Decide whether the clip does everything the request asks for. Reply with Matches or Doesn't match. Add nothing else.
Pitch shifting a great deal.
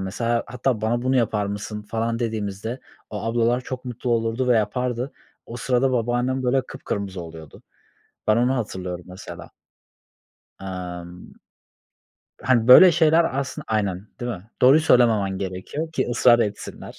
Doesn't match